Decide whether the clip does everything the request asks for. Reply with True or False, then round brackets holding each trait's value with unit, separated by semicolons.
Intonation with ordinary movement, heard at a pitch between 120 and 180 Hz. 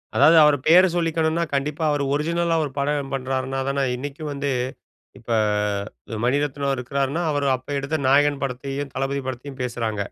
False (1.9 semitones; 140 Hz)